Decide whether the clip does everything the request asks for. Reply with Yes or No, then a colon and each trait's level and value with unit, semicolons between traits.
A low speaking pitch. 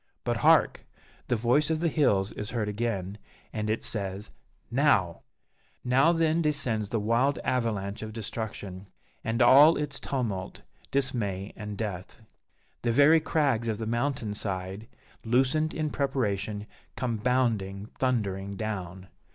Yes: low, 115 Hz